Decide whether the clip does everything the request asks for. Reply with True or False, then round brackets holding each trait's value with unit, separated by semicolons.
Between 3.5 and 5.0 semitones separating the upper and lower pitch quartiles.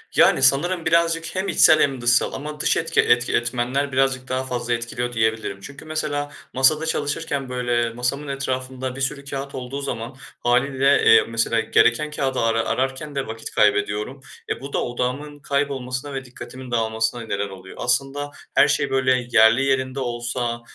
False (2.8 semitones)